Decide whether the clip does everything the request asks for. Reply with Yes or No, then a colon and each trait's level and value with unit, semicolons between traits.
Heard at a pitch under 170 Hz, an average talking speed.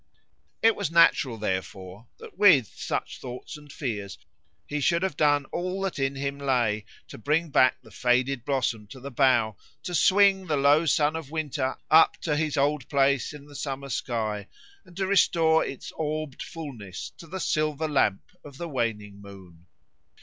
Yes: medium, 140 Hz; average, 170 wpm